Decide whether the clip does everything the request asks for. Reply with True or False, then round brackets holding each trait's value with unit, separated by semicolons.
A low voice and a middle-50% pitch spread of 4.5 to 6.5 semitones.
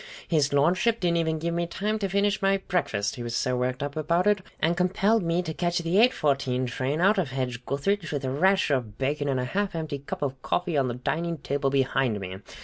False (155 Hz; 5.3 semitones)